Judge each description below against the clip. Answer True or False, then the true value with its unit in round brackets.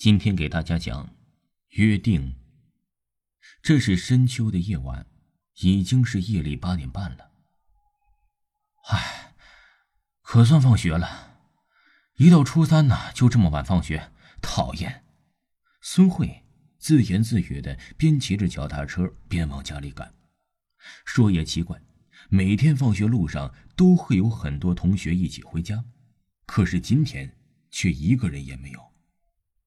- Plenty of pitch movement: True (7.4 semitones)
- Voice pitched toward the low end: True (95 Hz)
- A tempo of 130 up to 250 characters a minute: True (190 characters per minute)